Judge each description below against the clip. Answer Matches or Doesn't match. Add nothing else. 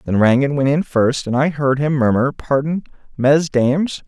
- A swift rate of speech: Doesn't match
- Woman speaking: Doesn't match